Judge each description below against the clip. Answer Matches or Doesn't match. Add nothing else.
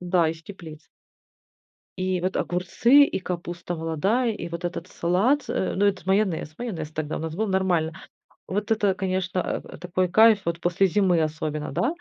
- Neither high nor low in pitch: Matches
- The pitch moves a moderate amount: Matches